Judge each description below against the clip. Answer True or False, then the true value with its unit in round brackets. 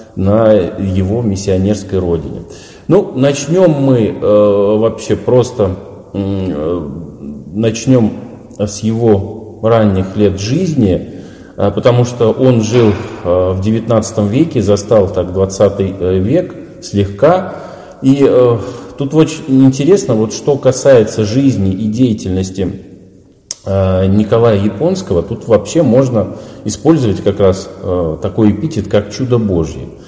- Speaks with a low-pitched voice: True (105 Hz)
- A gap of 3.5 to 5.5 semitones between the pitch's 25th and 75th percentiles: True (4.0 semitones)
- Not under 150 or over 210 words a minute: False (115 wpm)